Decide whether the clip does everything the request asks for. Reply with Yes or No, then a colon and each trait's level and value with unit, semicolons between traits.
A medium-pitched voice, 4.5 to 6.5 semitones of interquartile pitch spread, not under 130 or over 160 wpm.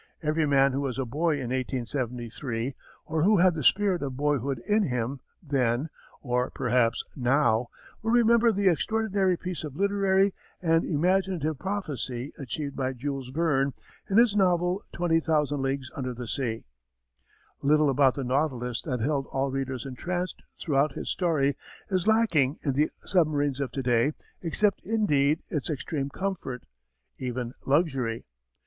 Yes: medium, 145 Hz; average, 5.2 semitones; average, 150 wpm